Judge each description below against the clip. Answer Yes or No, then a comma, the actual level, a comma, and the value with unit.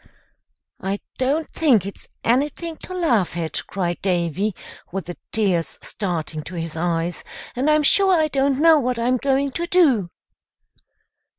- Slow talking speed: No, average, 150 wpm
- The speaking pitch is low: No, high, 235 Hz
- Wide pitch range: Yes, wide, 8.9 semitones